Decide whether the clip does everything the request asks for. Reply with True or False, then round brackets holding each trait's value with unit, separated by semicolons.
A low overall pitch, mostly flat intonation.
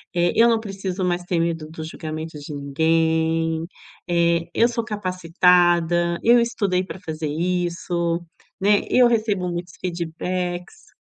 False (175 Hz; 2.3 semitones)